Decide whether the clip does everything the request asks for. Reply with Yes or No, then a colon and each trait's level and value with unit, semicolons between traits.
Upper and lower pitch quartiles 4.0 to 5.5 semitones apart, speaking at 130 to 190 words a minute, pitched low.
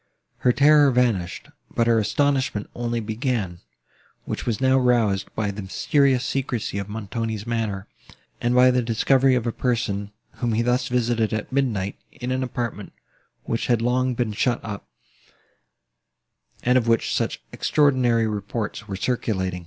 No: average, 2.9 semitones; average, 150 wpm; low, 120 Hz